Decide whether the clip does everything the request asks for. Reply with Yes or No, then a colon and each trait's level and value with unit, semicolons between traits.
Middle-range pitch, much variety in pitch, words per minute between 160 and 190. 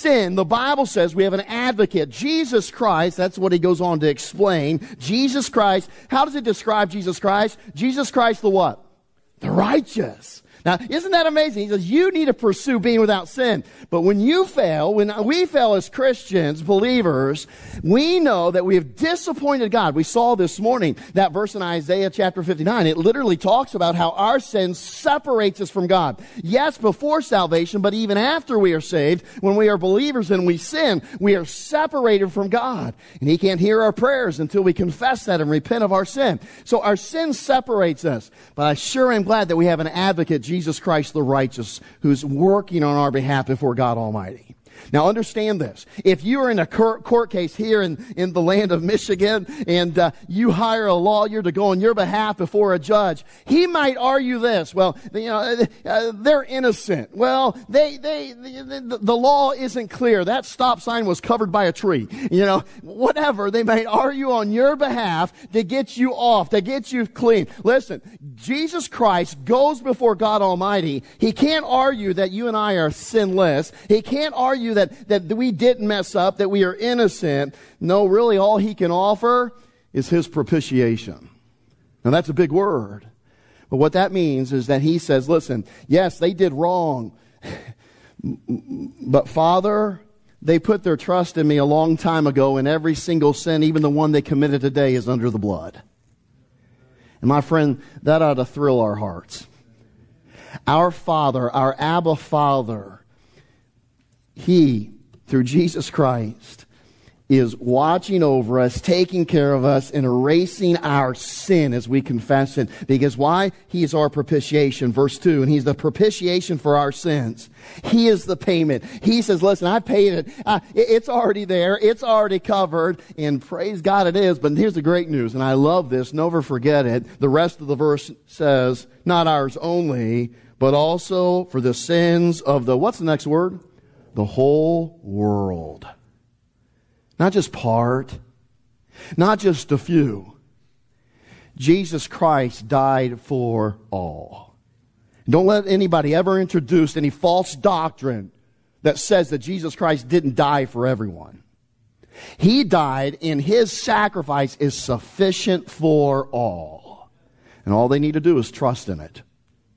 Yes: medium, 175 Hz; wide, 7.4 semitones; average, 170 wpm